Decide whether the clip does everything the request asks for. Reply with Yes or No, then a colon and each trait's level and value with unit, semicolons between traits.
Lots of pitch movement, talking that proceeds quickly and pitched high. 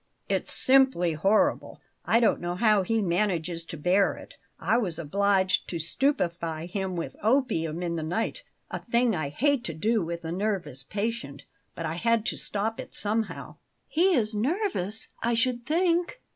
No: wide, 5.7 semitones; average, 170 wpm; high, 205 Hz